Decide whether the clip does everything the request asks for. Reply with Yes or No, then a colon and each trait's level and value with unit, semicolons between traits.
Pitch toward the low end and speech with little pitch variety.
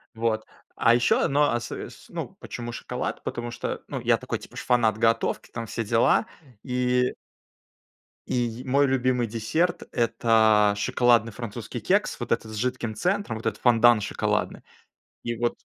Yes: low, 120 Hz; narrow, 1.8 semitones